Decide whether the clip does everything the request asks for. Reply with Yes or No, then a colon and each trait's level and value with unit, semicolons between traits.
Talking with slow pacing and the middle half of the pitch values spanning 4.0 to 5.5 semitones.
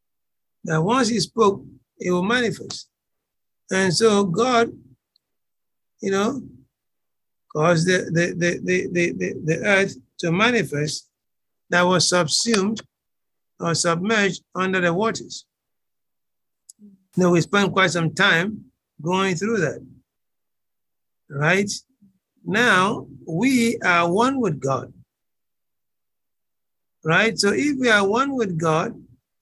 Yes: slow, 110 wpm; average, 4.3 semitones